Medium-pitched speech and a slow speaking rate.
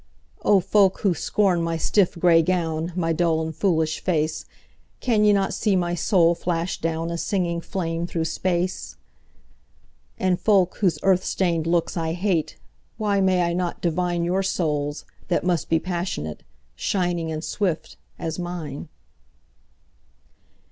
Yes: medium, 175 Hz; slow, 125 wpm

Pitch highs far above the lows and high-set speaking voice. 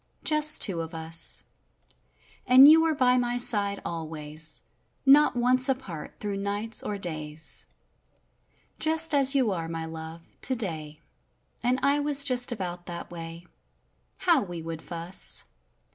Yes: wide, 7.9 semitones; high, 200 Hz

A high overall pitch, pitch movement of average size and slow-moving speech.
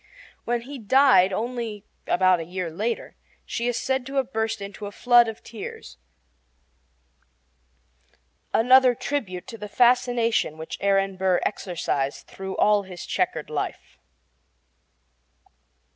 Yes: high, 215 Hz; average, 4.4 semitones; slow, 125 wpm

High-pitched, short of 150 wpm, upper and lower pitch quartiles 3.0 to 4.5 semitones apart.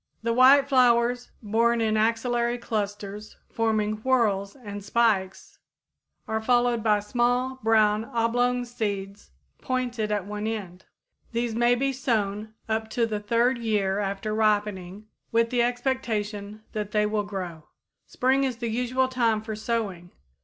No: high, 220 Hz; average, 140 wpm; narrow, 2.6 semitones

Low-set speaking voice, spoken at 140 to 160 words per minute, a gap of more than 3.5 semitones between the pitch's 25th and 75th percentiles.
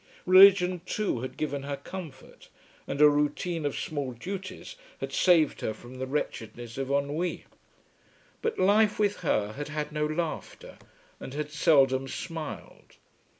No: medium, 150 Hz; average, 145 wpm; average, 4.9 semitones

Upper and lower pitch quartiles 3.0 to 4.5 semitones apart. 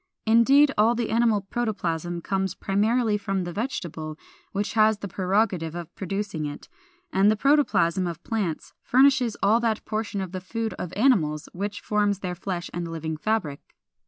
Yes: average, 4.2 semitones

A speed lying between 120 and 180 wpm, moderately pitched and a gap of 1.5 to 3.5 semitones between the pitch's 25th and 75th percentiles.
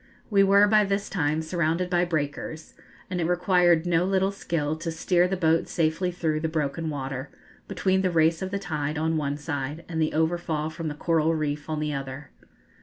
No: average, 195 wpm; medium, 160 Hz; narrow, 2.6 semitones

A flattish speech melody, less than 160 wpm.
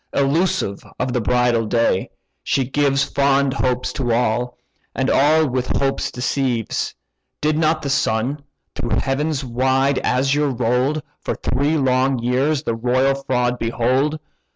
Yes: narrow, 2.3 semitones; slow, 135 wpm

